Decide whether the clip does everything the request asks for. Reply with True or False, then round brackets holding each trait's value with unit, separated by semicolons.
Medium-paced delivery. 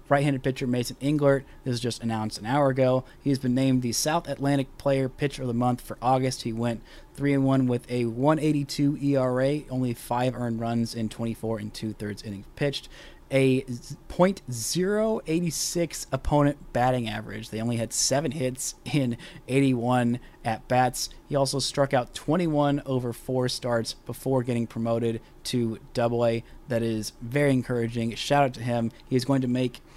True (165 wpm)